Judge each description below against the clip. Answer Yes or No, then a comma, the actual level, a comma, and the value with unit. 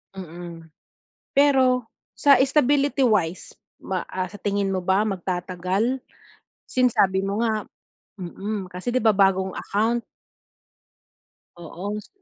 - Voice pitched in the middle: No, high, 200 Hz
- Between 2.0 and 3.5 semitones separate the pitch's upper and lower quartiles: No, average, 4.4 semitones